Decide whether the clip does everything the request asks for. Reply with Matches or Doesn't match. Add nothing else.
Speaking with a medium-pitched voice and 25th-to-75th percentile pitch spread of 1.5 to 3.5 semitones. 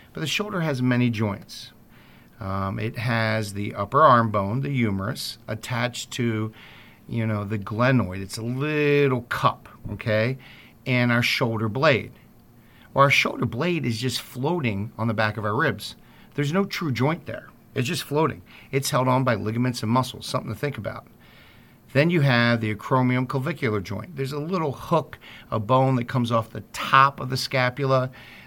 Doesn't match